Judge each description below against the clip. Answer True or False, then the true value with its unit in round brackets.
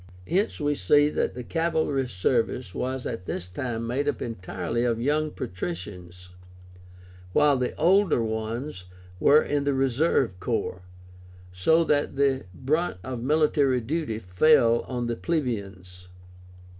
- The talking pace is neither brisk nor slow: False (130 wpm)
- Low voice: True (125 Hz)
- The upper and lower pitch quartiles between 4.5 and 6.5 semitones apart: True (5.3 semitones)